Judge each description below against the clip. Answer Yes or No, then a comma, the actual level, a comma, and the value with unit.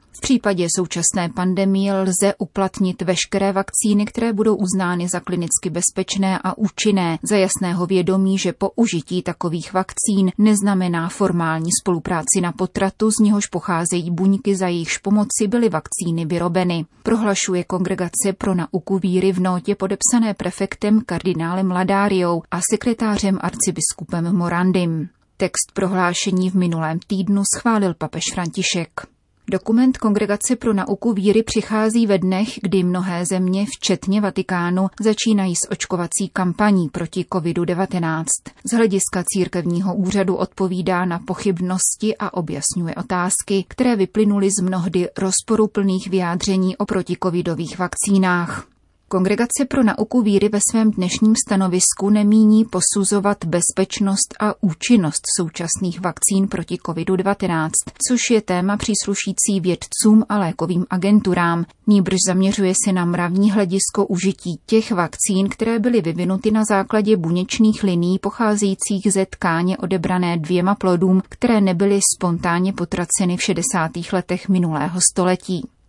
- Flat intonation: Yes, narrow, 2.3 semitones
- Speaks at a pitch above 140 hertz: Yes, high, 190 Hz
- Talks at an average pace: Yes, average, 125 wpm